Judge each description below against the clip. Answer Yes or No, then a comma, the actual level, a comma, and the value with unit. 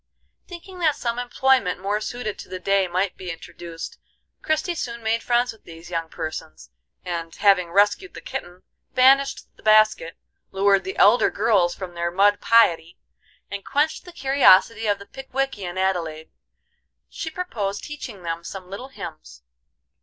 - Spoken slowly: No, average, 155 wpm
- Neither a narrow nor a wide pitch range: No, wide, 5.7 semitones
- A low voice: No, high, 200 Hz